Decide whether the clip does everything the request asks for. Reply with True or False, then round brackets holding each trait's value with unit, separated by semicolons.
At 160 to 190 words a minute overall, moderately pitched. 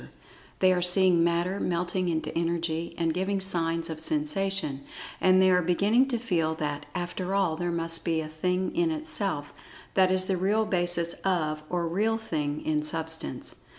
True (170 wpm; 175 Hz)